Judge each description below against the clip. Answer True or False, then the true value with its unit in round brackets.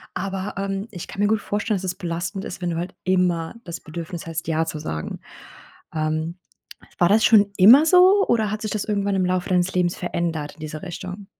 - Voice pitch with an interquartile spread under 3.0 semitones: False (3.3 semitones)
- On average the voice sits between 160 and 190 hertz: True (185 Hz)